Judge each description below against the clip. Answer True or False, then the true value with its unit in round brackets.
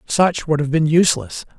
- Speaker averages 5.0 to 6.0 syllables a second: True (5.2 syllables/s)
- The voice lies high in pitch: False (160 Hz)